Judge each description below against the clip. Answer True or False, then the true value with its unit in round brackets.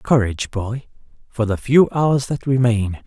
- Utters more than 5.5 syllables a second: False (4.3 syllables/s)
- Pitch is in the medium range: False (120 Hz)